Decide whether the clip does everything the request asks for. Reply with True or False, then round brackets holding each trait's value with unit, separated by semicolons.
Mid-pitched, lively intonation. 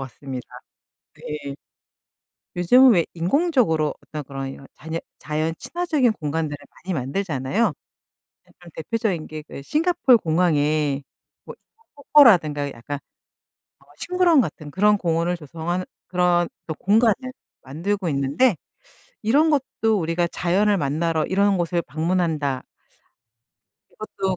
True (170 Hz; 5.9 semitones)